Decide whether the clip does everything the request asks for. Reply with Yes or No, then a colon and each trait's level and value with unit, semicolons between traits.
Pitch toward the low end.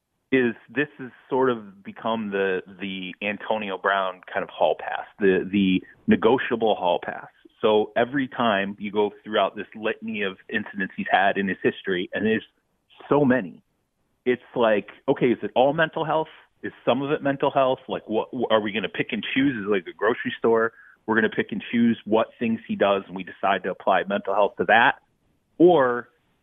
Yes: low, 115 Hz